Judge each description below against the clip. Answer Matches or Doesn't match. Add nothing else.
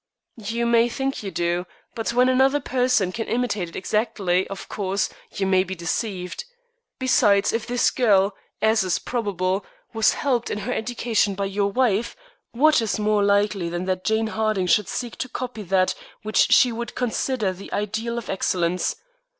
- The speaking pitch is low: Doesn't match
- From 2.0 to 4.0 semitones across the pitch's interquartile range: Matches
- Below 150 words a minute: Doesn't match